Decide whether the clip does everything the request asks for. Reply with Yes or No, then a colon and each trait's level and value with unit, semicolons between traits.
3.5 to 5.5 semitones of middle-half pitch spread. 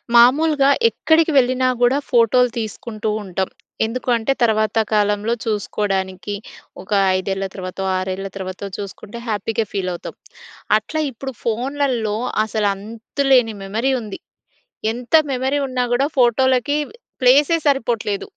Yes: average, 4.0 semitones